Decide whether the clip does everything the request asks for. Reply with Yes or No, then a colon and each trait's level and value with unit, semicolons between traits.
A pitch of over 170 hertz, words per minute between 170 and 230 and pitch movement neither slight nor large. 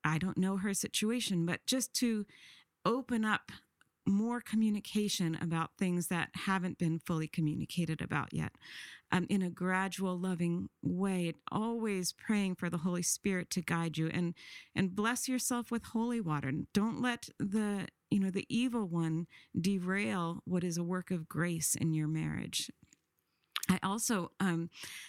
No: medium, 185 Hz; average, 155 wpm; average, 3.8 semitones